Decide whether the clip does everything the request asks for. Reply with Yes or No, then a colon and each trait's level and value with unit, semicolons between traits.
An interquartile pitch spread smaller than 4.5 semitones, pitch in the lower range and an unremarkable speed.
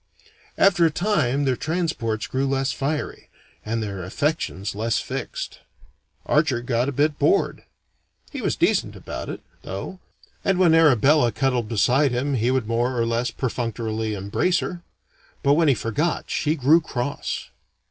No: average, 4.9 semitones; low, 130 Hz; average, 150 wpm